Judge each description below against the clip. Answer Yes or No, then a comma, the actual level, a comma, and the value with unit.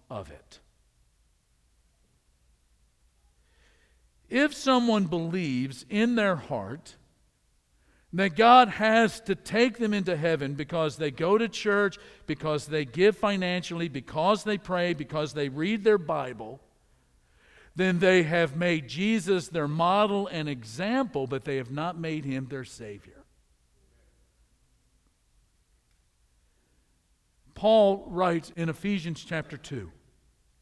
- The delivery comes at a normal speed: No, slow, 110 wpm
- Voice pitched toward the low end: No, medium, 155 Hz